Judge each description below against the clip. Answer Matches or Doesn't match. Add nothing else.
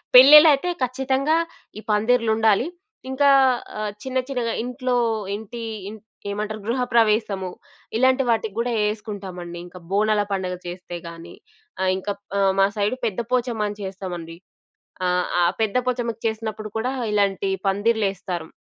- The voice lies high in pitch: Matches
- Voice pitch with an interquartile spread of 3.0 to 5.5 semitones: Matches